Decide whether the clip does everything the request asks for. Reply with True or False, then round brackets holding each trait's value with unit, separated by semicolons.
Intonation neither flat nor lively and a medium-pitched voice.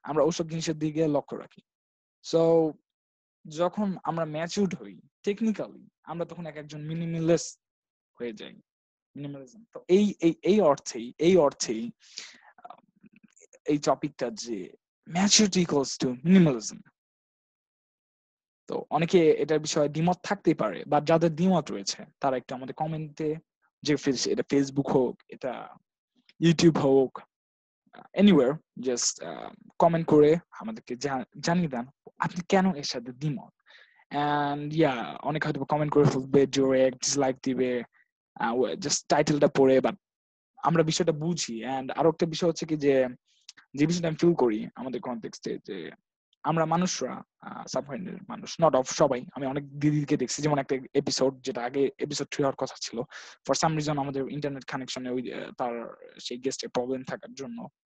True (3.9 semitones; 150 Hz)